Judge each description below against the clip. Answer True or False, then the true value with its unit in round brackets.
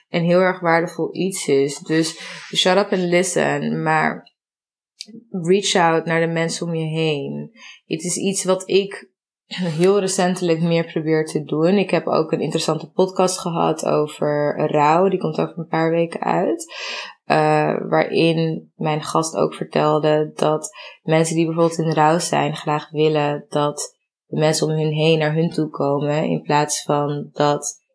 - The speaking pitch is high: False (165 Hz)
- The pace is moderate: True (165 wpm)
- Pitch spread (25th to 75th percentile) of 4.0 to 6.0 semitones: False (3.1 semitones)